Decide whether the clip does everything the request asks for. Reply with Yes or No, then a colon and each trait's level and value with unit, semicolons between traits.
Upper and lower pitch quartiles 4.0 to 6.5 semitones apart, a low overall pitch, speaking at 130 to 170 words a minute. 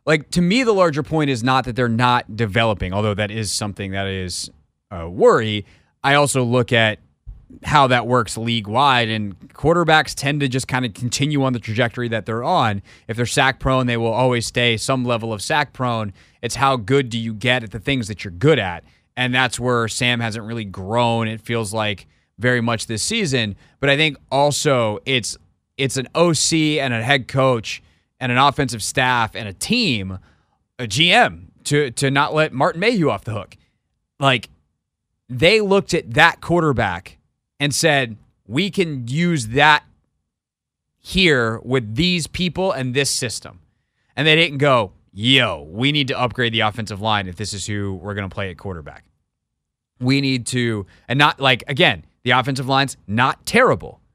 No: average, 4.5 semitones; low, 125 Hz; average, 185 wpm